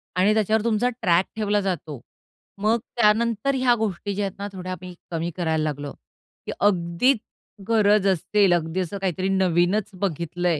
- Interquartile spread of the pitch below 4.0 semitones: Yes, average, 3.4 semitones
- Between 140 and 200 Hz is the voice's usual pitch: Yes, high, 190 Hz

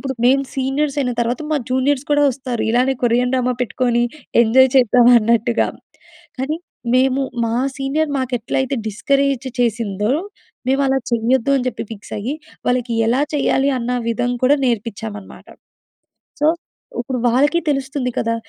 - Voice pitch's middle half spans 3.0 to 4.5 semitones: No, narrow, 2.5 semitones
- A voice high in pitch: Yes, very high, 255 Hz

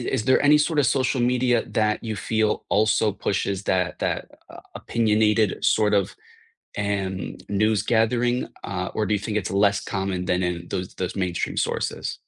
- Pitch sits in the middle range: No, low, 105 Hz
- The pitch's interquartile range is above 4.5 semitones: No, average, 2.9 semitones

